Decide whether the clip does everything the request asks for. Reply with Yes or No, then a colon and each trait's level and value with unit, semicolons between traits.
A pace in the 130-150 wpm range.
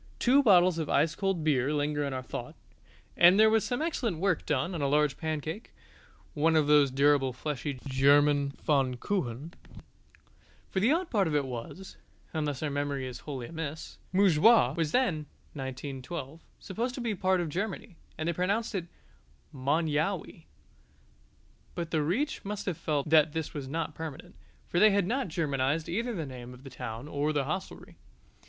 No: average, 175 wpm